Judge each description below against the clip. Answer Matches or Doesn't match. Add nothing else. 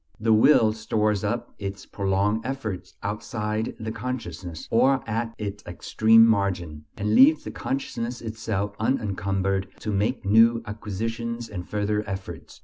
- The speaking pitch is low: Matches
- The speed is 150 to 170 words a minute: Doesn't match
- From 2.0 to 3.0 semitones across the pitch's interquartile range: Matches